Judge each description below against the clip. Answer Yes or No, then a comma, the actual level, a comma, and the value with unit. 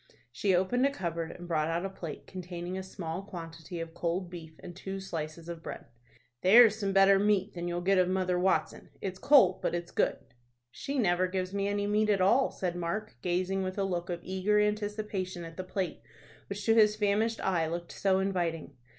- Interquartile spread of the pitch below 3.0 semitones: Yes, narrow, 2.6 semitones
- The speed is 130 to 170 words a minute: No, average, 200 wpm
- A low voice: No, medium, 185 Hz